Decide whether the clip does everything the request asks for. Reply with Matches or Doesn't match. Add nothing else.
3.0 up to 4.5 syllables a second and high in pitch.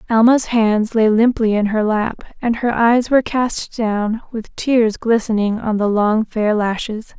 Matches